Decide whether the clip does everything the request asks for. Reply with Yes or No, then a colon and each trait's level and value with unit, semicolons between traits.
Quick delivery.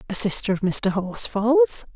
No: average, 155 wpm